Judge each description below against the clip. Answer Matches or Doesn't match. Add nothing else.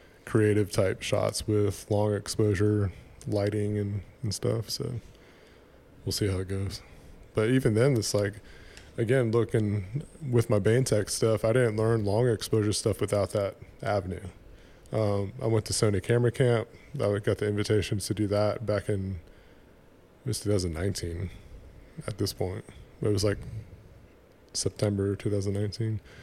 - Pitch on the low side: Matches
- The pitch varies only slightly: Matches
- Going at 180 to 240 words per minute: Doesn't match